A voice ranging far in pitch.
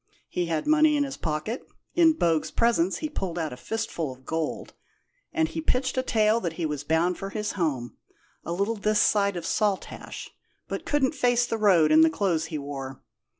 Yes: wide, 6.7 semitones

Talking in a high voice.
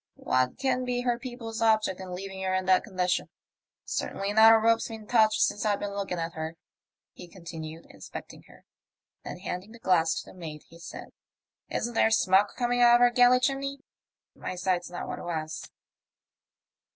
Yes: high, 200 Hz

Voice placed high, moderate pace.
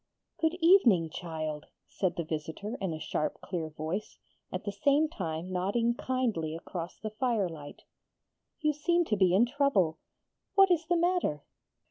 Yes: high, 200 Hz; average, 150 wpm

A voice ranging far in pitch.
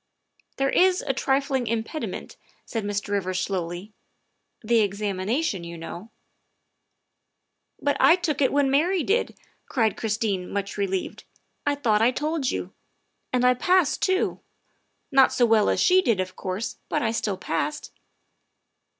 Yes: wide, 6.2 semitones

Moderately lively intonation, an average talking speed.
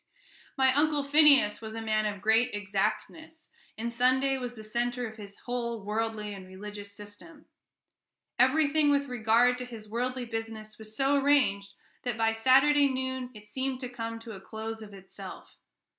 Yes: average, 3.4 semitones; average, 165 wpm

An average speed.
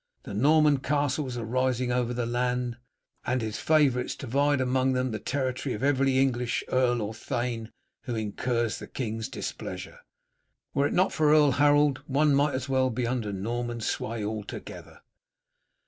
Yes: average, 160 wpm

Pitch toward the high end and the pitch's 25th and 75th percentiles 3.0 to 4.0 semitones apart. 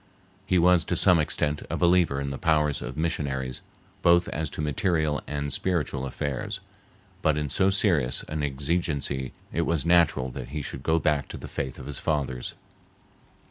No: very low, 75 Hz; average, 3.3 semitones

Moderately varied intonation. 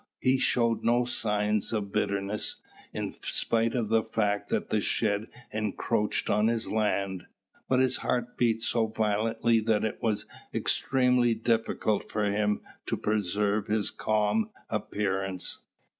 No: narrow, 1.9 semitones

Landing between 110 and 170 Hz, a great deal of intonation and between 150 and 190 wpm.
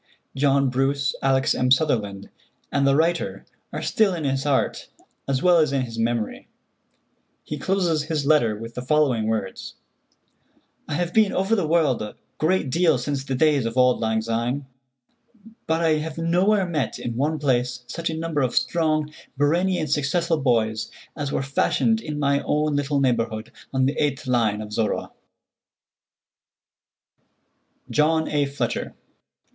No: medium, 140 Hz; average, 4.2 semitones; average, 155 wpm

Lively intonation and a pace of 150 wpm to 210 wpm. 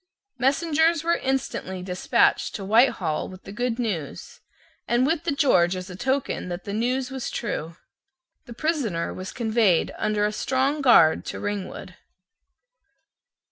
No: wide, 6.3 semitones; average, 140 wpm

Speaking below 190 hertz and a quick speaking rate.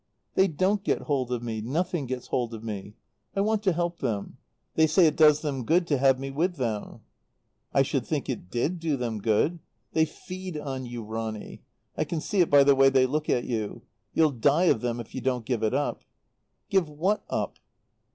Yes: medium, 140 Hz; fast, 210 wpm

